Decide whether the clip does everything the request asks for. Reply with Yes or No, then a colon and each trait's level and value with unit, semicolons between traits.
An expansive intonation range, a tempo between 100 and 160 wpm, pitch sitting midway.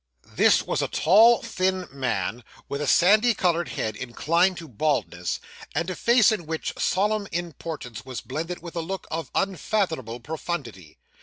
Yes: wide, 6.2 semitones; average, 155 wpm; medium, 165 Hz